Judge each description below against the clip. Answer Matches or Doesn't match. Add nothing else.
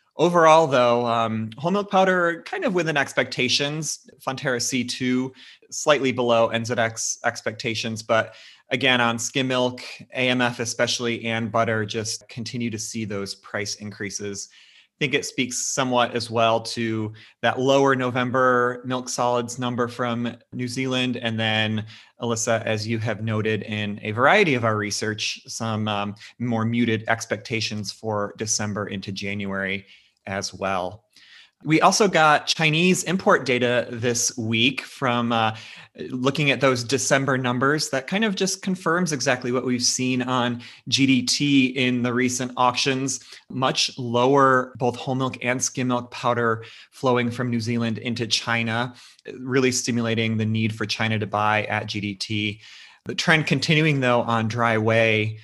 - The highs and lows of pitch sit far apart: Doesn't match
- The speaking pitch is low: Matches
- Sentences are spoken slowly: Doesn't match